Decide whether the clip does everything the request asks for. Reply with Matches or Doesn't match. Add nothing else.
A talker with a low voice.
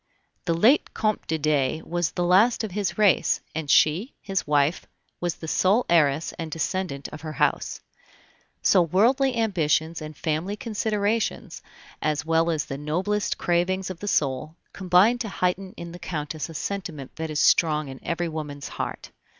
Doesn't match